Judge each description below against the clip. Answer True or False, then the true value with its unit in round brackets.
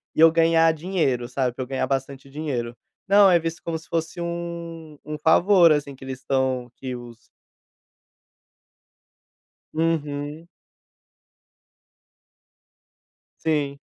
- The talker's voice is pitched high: False (150 Hz)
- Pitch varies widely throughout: False (3.8 semitones)